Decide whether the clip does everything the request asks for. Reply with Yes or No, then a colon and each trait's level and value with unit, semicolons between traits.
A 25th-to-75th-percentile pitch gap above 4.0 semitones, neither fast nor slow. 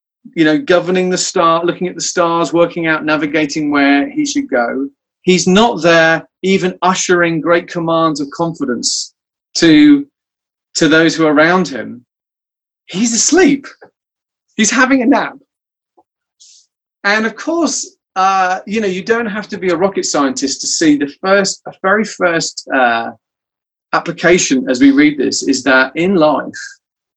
Yes: wide, 5.5 semitones; average, 150 wpm